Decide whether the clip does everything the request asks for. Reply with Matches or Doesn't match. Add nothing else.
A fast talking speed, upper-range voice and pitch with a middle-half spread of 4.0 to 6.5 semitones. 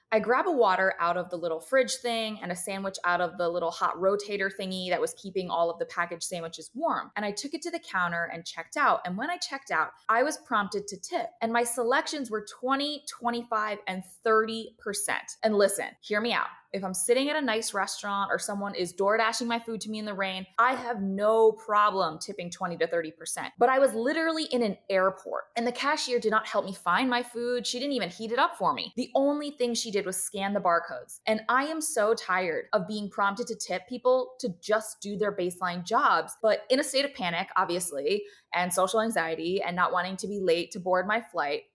Matches